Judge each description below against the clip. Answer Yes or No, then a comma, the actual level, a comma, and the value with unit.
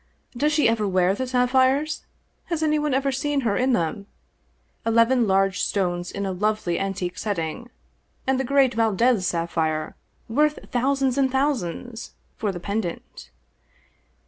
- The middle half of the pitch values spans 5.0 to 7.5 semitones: Yes, wide, 5.6 semitones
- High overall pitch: Yes, high, 230 Hz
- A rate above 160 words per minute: No, average, 145 wpm